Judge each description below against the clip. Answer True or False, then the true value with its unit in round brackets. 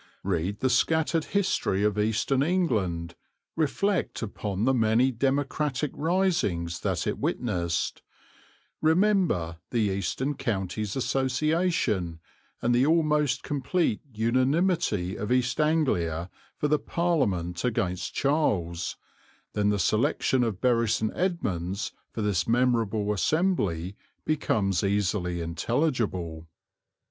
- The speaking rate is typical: False (105 wpm)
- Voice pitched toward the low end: True (115 Hz)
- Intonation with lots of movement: True (7.7 semitones)